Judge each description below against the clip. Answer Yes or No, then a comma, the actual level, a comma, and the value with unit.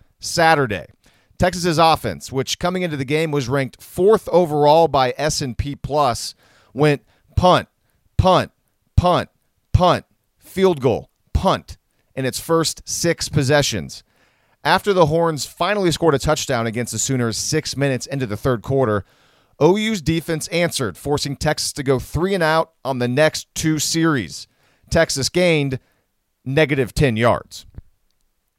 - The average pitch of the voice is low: No, medium, 145 Hz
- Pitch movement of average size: Yes, average, 4.8 semitones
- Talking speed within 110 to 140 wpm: Yes, slow, 135 wpm